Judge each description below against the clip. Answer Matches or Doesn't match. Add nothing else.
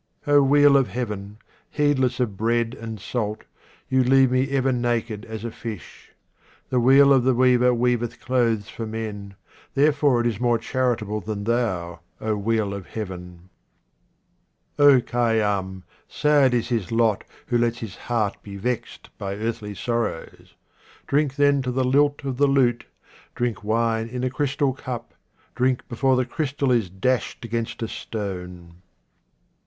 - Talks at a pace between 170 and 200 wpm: Doesn't match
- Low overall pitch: Matches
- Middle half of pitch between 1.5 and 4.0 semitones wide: Matches